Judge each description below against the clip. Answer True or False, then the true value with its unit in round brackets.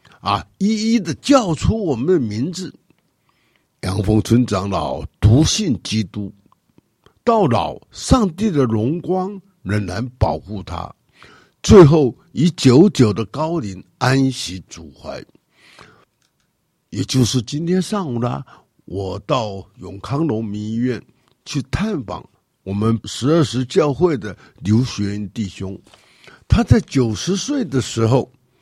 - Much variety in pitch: True (7.1 semitones)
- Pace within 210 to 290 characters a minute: False (175 characters per minute)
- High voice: False (125 Hz)